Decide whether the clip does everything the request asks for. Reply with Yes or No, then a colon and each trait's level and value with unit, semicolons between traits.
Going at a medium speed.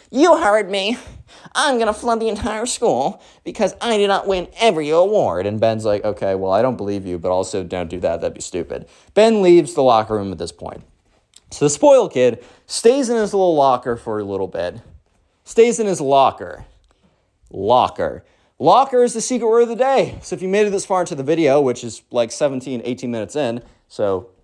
No: fast, 210 wpm